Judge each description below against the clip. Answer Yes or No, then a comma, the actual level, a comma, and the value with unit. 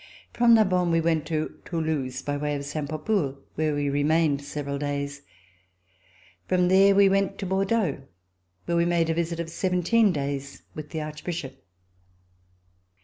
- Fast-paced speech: No, average, 150 wpm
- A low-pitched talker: No, medium, 160 Hz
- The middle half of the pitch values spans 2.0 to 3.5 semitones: No, average, 4.0 semitones